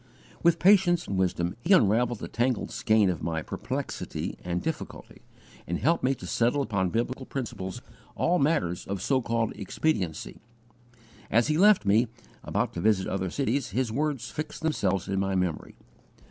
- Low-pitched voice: Yes, low, 115 Hz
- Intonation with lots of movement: Yes, wide, 7.0 semitones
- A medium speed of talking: Yes, average, 160 wpm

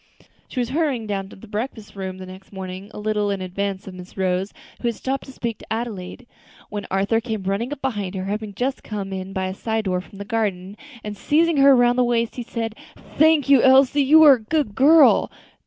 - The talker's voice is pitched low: No, high, 215 Hz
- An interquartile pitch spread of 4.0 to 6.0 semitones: Yes, average, 4.7 semitones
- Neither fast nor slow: No, fast, 225 wpm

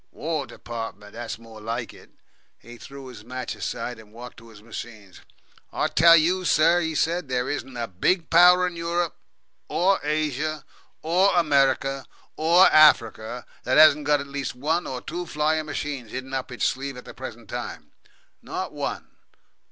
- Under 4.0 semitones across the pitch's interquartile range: No, average, 4.9 semitones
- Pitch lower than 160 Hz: Yes, medium, 140 Hz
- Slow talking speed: No, average, 165 wpm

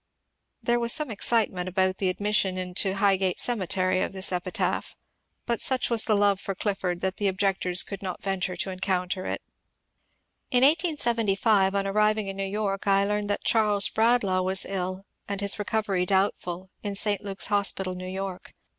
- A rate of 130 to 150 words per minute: No, average, 175 wpm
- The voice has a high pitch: Yes, high, 195 Hz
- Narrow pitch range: Yes, narrow, 2.1 semitones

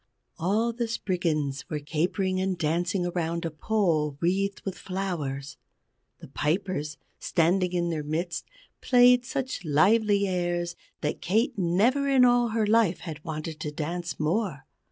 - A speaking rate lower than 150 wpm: Yes, average, 140 wpm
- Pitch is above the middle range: No, medium, 175 Hz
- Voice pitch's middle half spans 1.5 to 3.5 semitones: No, average, 4.8 semitones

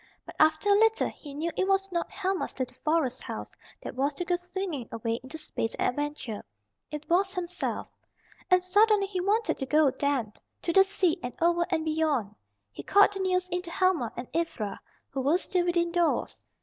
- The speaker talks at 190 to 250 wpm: Yes, average, 195 wpm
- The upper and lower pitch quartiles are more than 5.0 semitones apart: No, average, 4.7 semitones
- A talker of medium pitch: No, very high, 340 Hz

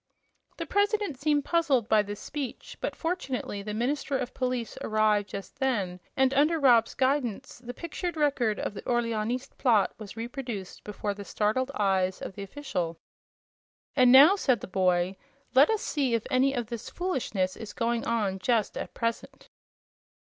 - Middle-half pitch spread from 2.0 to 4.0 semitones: No, average, 4.8 semitones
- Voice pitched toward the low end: No, high, 240 Hz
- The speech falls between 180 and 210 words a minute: No, average, 160 wpm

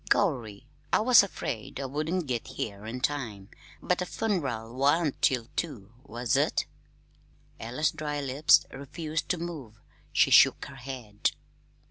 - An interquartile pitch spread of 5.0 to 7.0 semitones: Yes, average, 5.3 semitones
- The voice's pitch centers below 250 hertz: Yes, low, 135 Hz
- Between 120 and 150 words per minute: Yes, average, 140 wpm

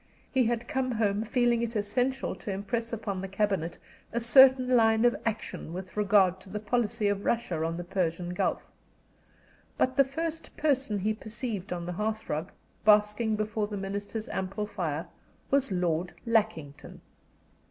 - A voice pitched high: Yes, high, 210 Hz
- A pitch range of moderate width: Yes, average, 3.7 semitones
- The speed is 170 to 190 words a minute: No, average, 160 wpm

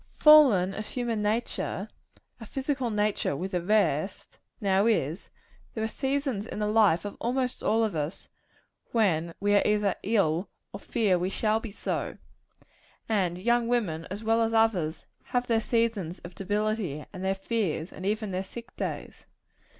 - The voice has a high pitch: Yes, high, 210 Hz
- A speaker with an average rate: Yes, average, 165 wpm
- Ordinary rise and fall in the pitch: Yes, average, 3.6 semitones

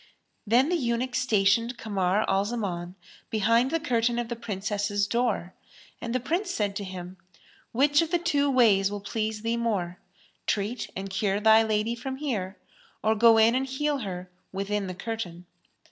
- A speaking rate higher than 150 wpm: Yes, average, 170 wpm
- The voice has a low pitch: No, high, 220 Hz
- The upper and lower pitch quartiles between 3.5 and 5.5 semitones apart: Yes, average, 3.8 semitones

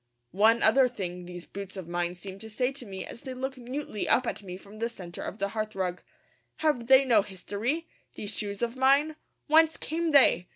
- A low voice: No, high, 220 Hz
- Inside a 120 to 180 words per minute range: No, fast, 205 wpm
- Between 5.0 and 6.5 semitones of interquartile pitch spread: Yes, wide, 5.5 semitones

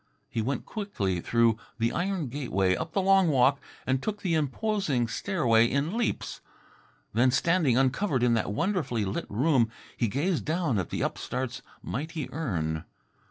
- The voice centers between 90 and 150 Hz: Yes, low, 135 Hz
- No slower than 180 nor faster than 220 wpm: No, average, 155 wpm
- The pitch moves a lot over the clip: Yes, wide, 6.5 semitones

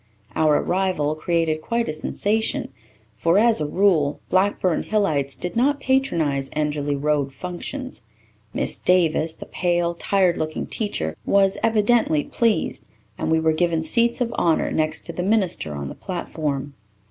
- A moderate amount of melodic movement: Yes, average, 5.0 semitones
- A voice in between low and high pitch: Yes, medium, 170 Hz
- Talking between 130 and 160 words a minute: Yes, average, 150 wpm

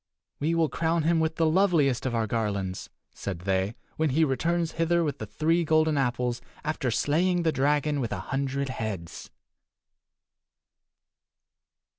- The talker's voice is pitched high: No, medium, 145 Hz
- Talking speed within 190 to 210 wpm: No, average, 145 wpm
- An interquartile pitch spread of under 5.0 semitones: No, wide, 5.5 semitones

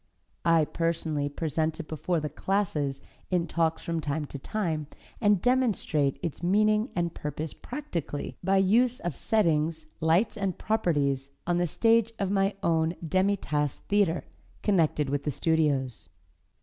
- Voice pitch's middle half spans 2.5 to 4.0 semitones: No, average, 4.7 semitones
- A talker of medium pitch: Yes, medium, 170 Hz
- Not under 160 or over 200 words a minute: No, average, 145 wpm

